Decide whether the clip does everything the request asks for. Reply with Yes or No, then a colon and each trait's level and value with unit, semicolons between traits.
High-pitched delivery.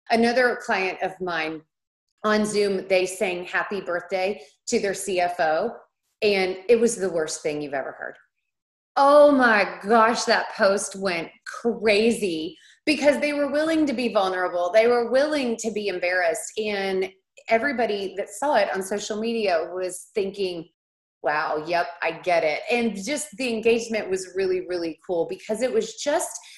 Yes: high, 200 Hz